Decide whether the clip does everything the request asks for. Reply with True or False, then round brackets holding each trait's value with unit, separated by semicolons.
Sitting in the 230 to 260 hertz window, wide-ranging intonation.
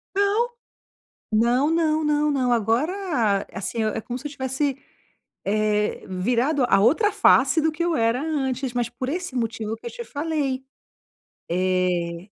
True (255 Hz; 5.7 semitones)